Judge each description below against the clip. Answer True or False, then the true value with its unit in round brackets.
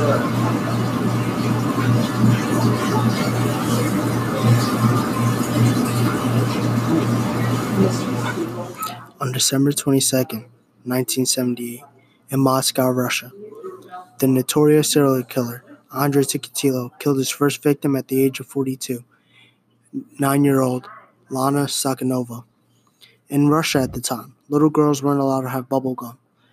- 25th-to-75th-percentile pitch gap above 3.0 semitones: False (2.7 semitones)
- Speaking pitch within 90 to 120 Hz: False (130 Hz)